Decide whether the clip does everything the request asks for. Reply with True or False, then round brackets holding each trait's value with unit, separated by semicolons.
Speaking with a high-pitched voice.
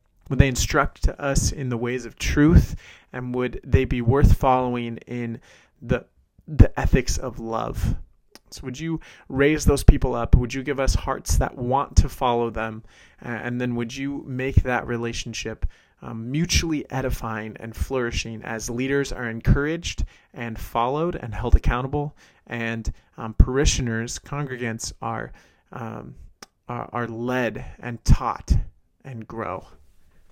False (120 Hz)